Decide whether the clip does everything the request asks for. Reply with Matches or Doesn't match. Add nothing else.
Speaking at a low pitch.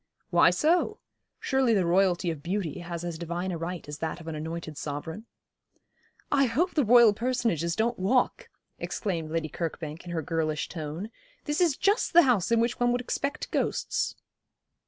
Doesn't match